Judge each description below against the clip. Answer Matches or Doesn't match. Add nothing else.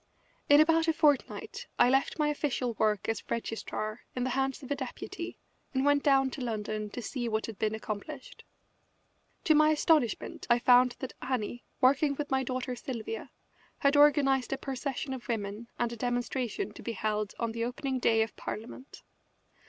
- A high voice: Matches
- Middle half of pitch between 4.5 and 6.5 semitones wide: Doesn't match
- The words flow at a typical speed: Matches